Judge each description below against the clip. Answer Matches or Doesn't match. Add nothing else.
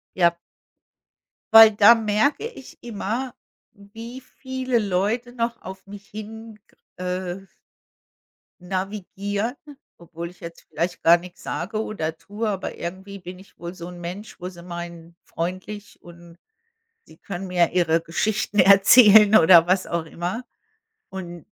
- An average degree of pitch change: Matches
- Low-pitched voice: Doesn't match